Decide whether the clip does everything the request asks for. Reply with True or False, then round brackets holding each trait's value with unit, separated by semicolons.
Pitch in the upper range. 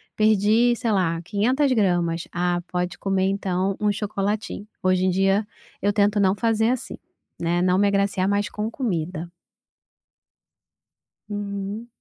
True (200 Hz)